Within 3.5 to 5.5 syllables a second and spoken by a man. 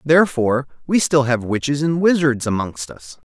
Yes: 5.1 syllables/s; male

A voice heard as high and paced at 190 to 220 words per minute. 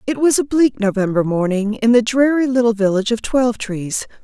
Yes: high, 230 Hz; average, 200 wpm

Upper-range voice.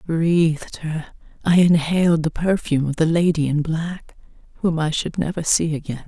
No: medium, 160 Hz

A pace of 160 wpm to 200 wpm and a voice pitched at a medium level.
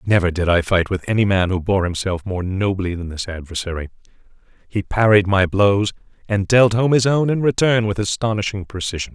No: average, 190 wpm; low, 100 Hz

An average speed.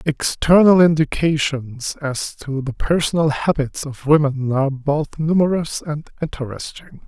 No: slow, 120 wpm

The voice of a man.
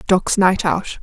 No: female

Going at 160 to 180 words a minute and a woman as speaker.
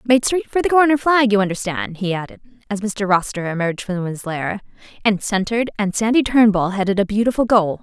No: average, 200 wpm; female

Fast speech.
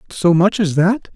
Yes: fast, 210 wpm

